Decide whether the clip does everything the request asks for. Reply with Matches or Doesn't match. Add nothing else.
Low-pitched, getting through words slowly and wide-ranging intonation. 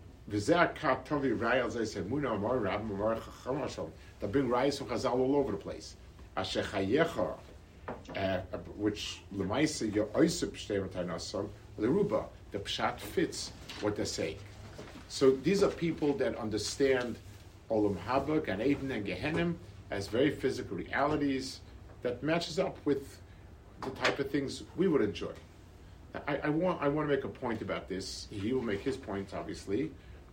Doesn't match